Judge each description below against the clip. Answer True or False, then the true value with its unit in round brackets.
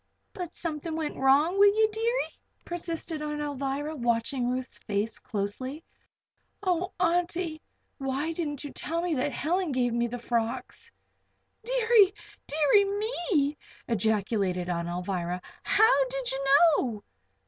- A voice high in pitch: True (295 Hz)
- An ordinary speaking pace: False (125 wpm)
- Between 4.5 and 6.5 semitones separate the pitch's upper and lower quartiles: False (6.9 semitones)